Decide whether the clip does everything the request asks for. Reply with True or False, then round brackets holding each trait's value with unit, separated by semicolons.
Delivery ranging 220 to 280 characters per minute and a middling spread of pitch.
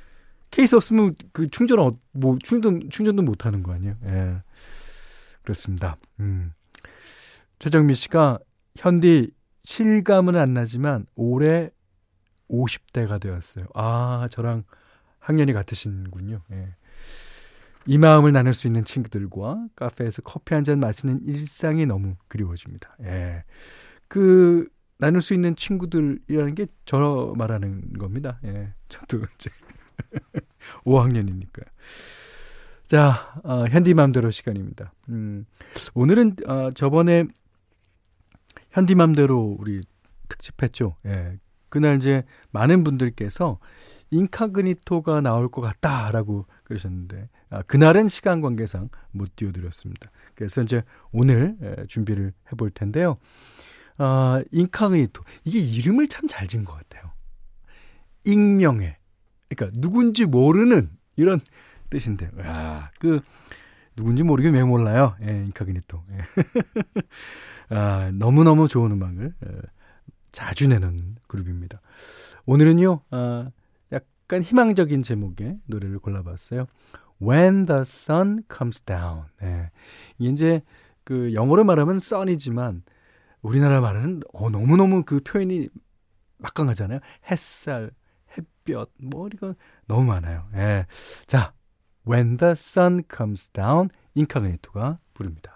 False (265 characters per minute; 7.5 semitones)